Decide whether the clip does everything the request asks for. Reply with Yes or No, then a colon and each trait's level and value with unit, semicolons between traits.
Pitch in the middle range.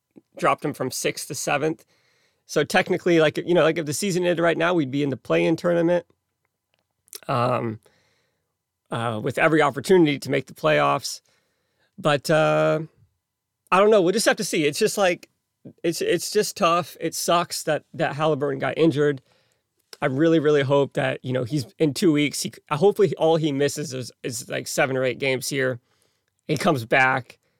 Yes: medium, 155 Hz